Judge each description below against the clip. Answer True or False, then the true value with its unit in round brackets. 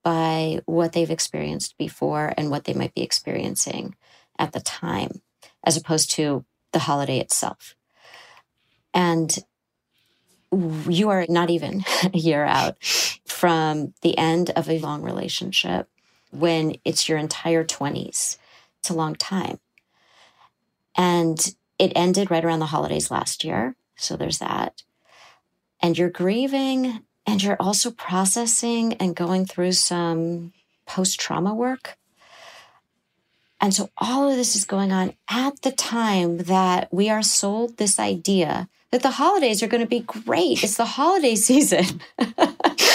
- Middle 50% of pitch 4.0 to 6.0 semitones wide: True (4.7 semitones)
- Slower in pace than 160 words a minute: True (140 wpm)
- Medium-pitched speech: True (180 Hz)